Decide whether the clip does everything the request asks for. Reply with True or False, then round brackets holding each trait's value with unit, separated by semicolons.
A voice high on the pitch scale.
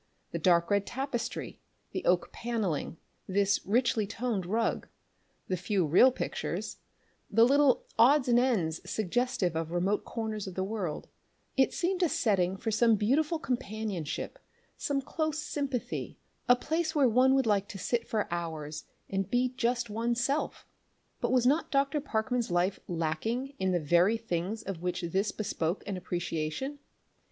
True (220 Hz)